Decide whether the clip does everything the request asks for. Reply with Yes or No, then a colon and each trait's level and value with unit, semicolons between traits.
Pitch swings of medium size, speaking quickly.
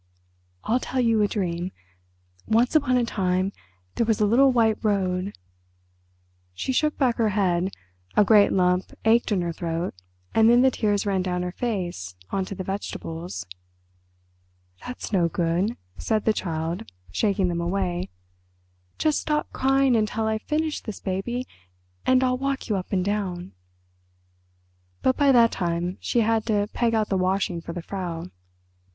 No: average, 4.5 semitones; average, 160 wpm